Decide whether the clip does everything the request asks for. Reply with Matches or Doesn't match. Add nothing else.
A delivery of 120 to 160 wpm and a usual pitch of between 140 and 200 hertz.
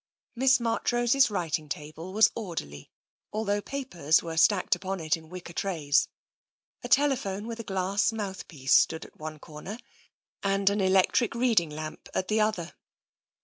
Matches